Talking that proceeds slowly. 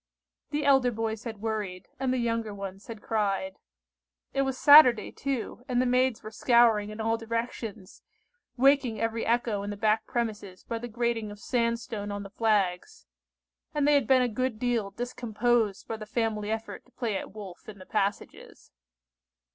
No: average, 180 wpm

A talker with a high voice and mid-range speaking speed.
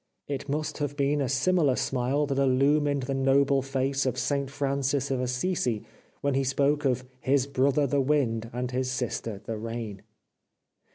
No: low, 135 Hz; average, 170 wpm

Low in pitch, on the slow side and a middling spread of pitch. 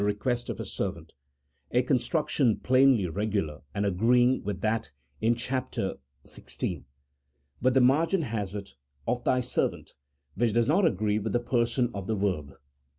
No: low, 115 Hz; average, 155 wpm; average, 3.9 semitones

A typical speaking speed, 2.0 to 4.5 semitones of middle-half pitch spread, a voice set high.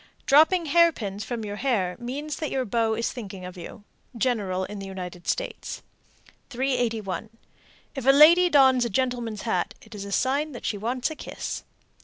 No: average, 175 wpm; average, 5.1 semitones; high, 240 Hz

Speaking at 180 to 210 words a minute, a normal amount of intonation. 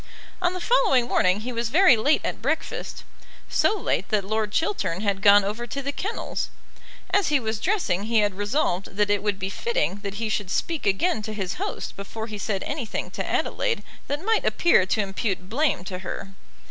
No: average, 200 wpm; wide, 6.5 semitones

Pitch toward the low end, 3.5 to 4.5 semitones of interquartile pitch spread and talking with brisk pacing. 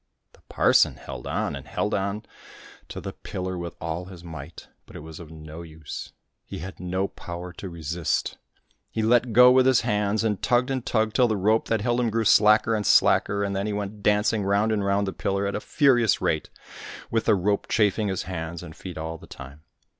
Yes: low, 100 Hz; average, 4.0 semitones; fast, 215 wpm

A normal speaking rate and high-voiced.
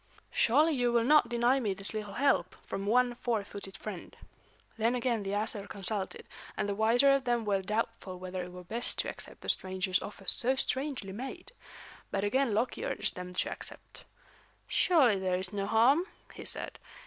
Yes: average, 185 wpm; high, 215 Hz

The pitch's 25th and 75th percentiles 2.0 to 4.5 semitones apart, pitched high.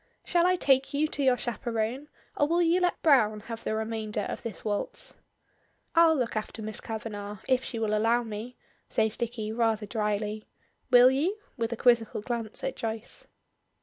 Yes: average, 3.4 semitones; high, 230 Hz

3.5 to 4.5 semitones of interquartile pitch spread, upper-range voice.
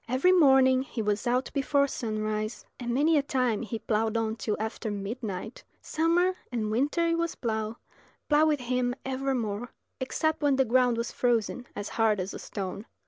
Yes: average, 3.9 semitones; high, 245 Hz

